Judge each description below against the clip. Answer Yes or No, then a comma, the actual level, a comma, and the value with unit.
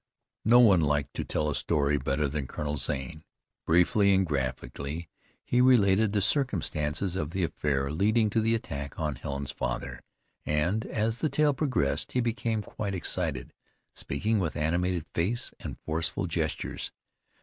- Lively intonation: Yes, wide, 6.8 semitones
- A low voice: Yes, very low, 85 Hz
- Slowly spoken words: No, average, 150 wpm